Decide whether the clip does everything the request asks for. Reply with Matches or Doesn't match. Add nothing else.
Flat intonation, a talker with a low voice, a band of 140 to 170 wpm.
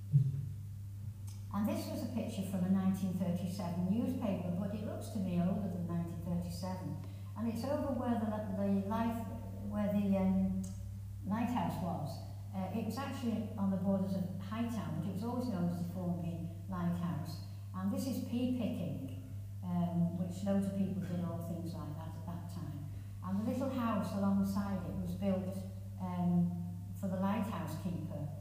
Matches